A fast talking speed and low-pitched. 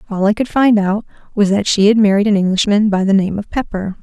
No: fast, 255 wpm; high, 205 Hz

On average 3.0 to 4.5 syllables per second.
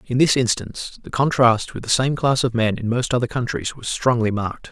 No: 5.6 syllables/s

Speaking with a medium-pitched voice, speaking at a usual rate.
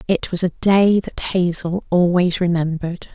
Yes: medium, 180 Hz; average, 155 wpm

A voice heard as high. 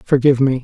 No: low, 135 Hz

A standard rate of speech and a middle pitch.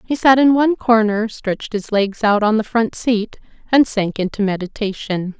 No: average, 190 wpm; high, 220 Hz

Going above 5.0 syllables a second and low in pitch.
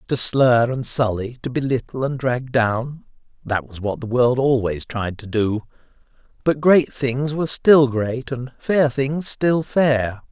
No: 3.9 syllables/s; low, 125 Hz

